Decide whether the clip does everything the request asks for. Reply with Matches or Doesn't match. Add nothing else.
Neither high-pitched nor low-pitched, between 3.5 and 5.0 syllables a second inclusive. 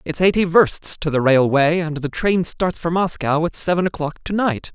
Matches